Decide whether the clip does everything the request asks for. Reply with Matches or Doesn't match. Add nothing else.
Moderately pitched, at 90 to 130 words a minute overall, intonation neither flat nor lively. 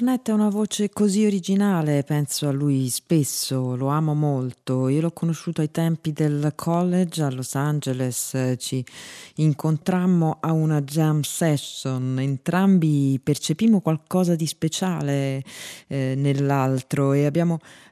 Matches